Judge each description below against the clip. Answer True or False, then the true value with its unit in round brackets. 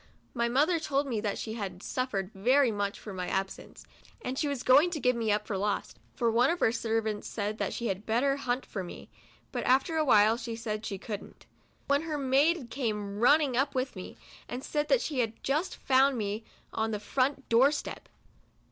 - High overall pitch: True (240 Hz)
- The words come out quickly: True (215 wpm)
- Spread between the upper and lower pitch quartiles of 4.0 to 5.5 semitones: True (4.6 semitones)